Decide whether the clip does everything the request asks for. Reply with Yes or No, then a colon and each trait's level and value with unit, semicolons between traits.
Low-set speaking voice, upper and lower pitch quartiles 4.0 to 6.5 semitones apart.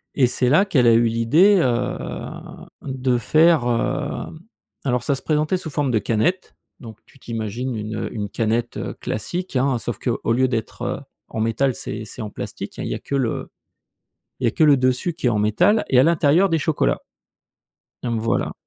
Yes: low, 125 Hz; average, 4.8 semitones